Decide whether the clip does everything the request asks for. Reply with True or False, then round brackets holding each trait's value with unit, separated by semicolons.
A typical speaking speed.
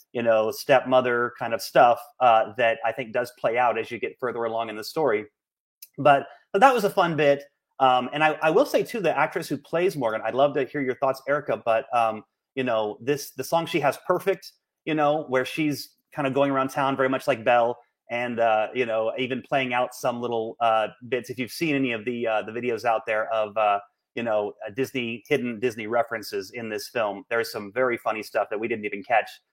False (230 wpm)